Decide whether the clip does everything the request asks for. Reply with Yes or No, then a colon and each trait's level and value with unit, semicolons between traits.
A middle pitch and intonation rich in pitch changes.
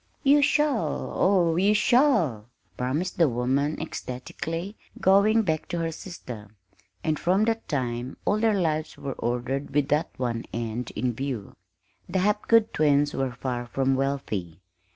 Yes: medium, 145 Hz; wide, 7.3 semitones